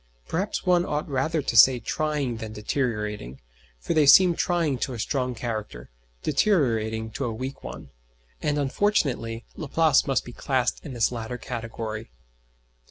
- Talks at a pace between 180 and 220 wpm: No, average, 150 wpm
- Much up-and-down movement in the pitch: No, average, 5.0 semitones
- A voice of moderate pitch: No, low, 130 Hz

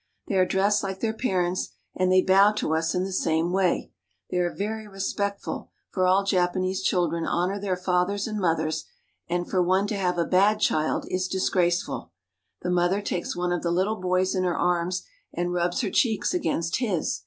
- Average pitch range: No, narrow, 2.0 semitones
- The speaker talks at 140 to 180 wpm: No, average, 190 wpm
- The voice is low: No, medium, 185 Hz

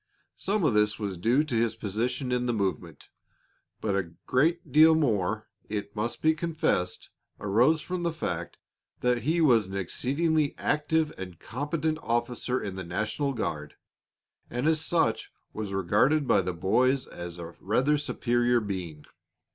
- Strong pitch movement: Yes, wide, 7.3 semitones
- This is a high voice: No, low, 120 Hz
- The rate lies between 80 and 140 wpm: No, average, 155 wpm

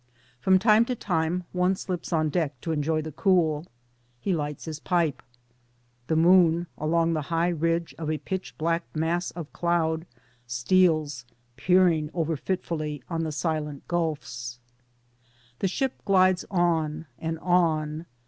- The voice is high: No, medium, 165 Hz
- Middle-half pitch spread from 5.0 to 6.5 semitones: No, narrow, 2.5 semitones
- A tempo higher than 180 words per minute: No, average, 140 wpm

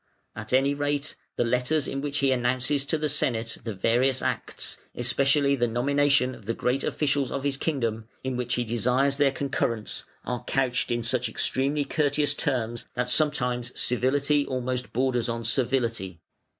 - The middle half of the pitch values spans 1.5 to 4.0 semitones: Yes, average, 2.7 semitones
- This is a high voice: No, low, 130 Hz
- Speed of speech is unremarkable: Yes, average, 165 wpm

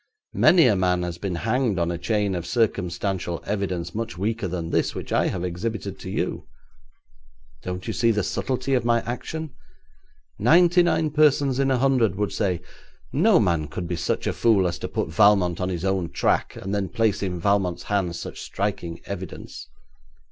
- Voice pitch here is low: Yes, low, 100 Hz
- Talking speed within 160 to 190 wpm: Yes, average, 185 wpm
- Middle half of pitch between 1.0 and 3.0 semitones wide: No, average, 4.7 semitones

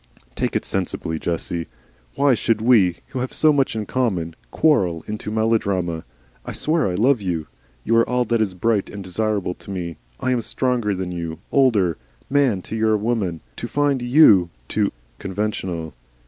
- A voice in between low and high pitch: No, low, 105 Hz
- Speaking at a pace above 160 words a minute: Yes, average, 170 wpm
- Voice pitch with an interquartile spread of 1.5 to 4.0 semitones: No, wide, 5.5 semitones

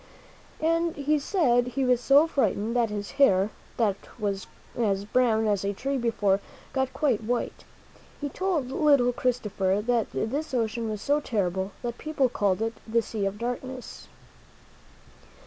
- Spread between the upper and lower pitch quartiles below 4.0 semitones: No, average, 4.5 semitones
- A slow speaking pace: No, average, 150 wpm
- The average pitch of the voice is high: Yes, high, 240 Hz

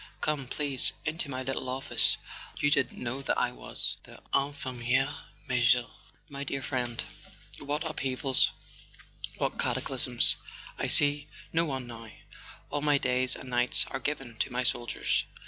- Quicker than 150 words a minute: No, average, 145 wpm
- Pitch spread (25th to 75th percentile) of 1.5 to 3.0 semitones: Yes, narrow, 2.4 semitones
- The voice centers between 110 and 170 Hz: Yes, low, 135 Hz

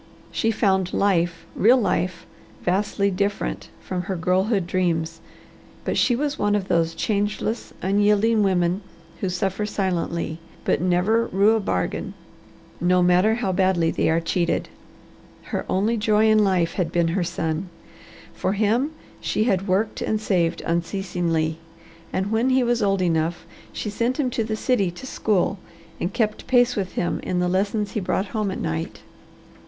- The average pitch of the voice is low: No, high, 195 Hz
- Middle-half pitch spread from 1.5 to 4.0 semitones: Yes, average, 3.4 semitones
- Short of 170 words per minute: Yes, average, 160 wpm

